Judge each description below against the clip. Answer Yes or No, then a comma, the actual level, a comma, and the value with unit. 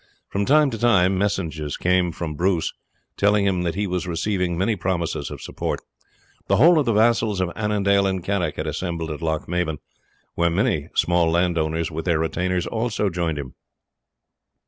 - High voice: No, very low, 90 Hz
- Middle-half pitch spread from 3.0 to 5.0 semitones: Yes, average, 3.3 semitones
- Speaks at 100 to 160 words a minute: No, average, 170 wpm